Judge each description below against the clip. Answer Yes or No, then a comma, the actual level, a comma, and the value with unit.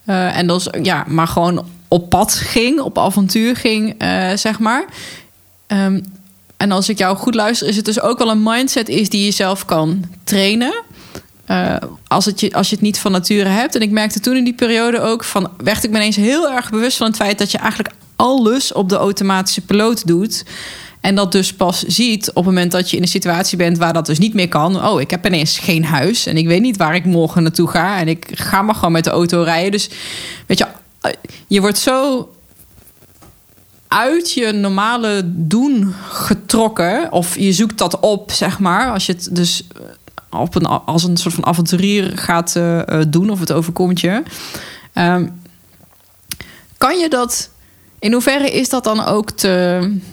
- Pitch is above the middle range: Yes, high, 195 Hz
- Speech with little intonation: No, average, 3.7 semitones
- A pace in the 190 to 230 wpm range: Yes, fast, 200 wpm